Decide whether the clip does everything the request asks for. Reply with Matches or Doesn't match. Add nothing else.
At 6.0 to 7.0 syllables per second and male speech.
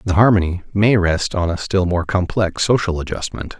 Doesn't match